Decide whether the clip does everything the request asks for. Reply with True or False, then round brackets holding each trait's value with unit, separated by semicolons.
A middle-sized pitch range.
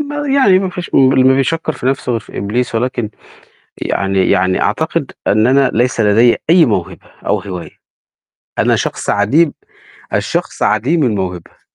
False (6.7 semitones)